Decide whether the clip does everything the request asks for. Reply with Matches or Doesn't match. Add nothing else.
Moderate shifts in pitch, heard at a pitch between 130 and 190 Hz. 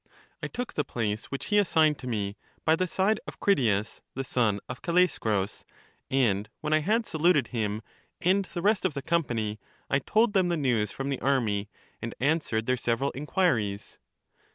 Doesn't match